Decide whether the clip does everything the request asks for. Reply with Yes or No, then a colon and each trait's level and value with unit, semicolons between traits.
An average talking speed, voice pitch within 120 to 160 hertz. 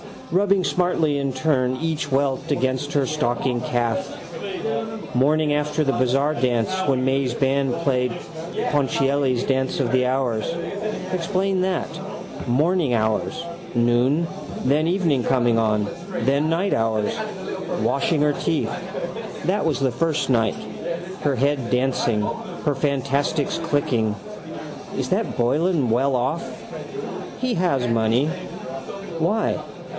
No: slow, 120 wpm; low, 135 Hz